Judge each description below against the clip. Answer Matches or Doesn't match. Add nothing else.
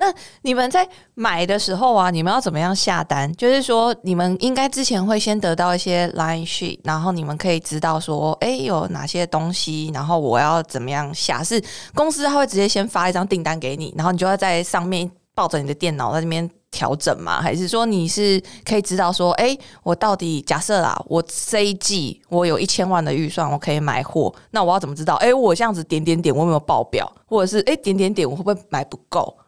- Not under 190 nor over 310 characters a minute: Doesn't match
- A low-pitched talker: Doesn't match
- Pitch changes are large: Doesn't match